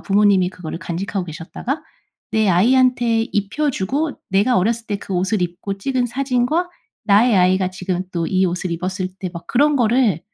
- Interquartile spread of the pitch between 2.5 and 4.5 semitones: No, average, 5.1 semitones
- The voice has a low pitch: No, high, 200 Hz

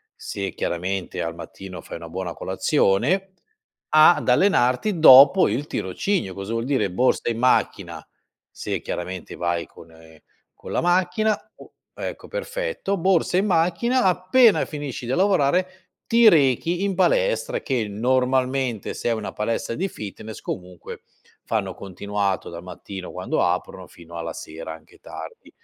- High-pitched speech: No, low, 125 Hz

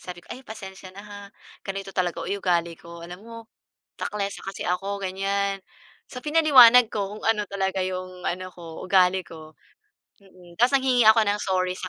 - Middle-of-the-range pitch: No, high, 195 Hz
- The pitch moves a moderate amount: No, narrow, 2.3 semitones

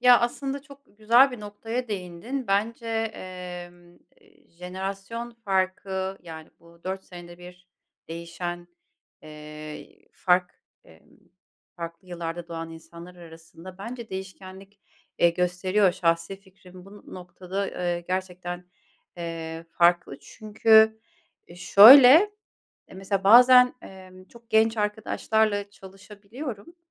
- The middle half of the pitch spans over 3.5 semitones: Yes, average, 3.9 semitones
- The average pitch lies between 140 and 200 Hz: Yes, high, 190 Hz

